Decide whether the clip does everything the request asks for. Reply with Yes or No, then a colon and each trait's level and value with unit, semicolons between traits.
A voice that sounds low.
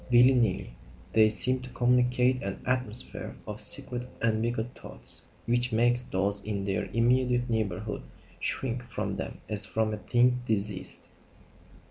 Yes: low, 120 Hz